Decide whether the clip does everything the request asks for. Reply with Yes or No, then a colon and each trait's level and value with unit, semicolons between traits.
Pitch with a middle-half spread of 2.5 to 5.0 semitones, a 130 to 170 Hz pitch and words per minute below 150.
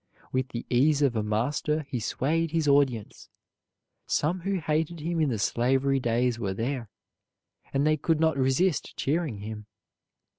No: average, 4.5 semitones; medium, 140 Hz; average, 155 wpm